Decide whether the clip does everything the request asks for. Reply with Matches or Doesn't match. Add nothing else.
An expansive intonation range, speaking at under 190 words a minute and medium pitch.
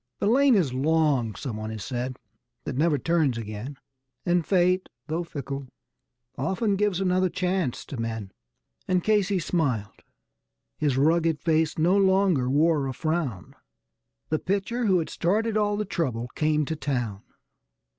Matches